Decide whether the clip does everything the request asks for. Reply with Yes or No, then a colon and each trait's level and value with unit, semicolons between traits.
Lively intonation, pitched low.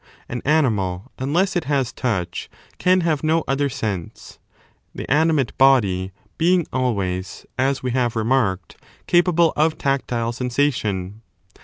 Yes: wide, 6.1 semitones; low, 130 Hz